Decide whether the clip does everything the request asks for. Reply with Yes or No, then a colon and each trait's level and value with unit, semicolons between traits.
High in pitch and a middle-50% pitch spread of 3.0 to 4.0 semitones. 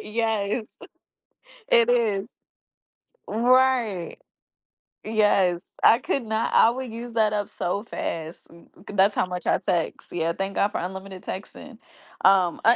Yes: high, 210 Hz; average, 3.5 semitones